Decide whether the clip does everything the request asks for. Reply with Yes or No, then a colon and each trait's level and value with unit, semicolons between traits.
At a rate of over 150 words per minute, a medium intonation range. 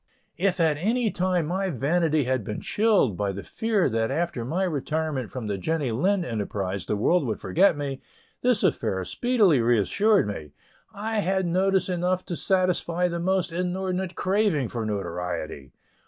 No: average, 160 wpm; wide, 8.5 semitones